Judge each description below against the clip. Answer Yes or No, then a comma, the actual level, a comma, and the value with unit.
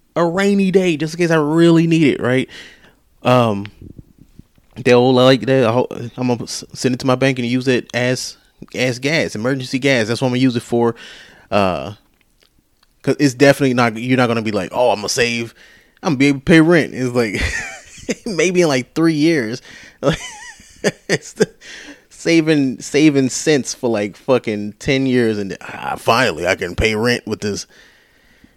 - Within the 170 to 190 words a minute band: Yes, average, 175 wpm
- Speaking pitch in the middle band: No, low, 130 Hz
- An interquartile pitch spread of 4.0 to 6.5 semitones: No, average, 3.5 semitones